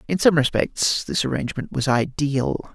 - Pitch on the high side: No, medium, 140 Hz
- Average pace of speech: Yes, average, 155 wpm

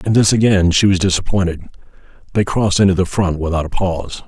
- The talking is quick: No, average, 195 wpm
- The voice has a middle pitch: No, very low, 95 Hz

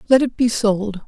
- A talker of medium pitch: No, high, 220 Hz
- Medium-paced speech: No, fast, 225 wpm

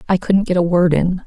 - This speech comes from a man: No, female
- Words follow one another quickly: Yes, fast, 285 wpm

